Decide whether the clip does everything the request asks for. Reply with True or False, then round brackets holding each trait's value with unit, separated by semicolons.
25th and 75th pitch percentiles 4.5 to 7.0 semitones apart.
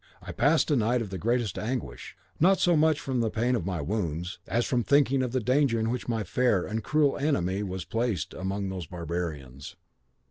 True (5.6 semitones)